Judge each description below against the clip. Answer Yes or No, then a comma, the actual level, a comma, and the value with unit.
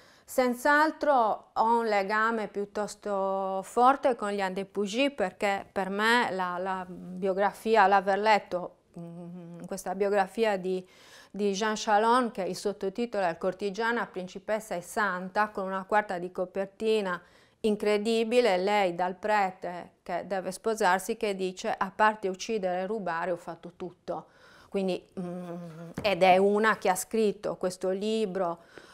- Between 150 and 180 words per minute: No, average, 135 wpm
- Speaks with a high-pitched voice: Yes, high, 195 Hz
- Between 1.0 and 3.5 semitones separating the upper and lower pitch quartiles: Yes, average, 2.7 semitones